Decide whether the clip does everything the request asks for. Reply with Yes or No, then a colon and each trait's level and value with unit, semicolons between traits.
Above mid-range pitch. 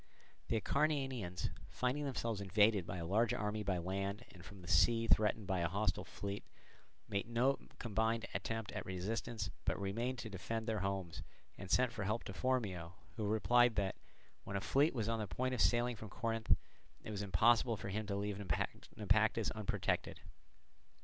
No: low, 105 Hz